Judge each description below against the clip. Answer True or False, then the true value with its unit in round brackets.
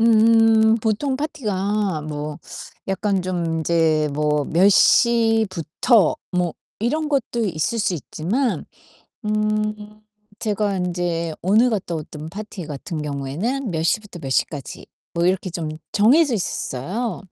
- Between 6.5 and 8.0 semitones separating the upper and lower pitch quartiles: False (5.3 semitones)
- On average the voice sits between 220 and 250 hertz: False (195 Hz)